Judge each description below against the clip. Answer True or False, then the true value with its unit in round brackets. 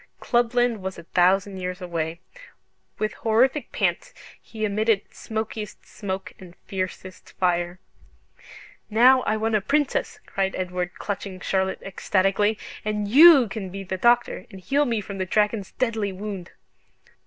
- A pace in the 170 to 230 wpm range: False (140 wpm)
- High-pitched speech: True (200 Hz)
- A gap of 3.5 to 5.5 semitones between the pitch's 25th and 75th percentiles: False (3.1 semitones)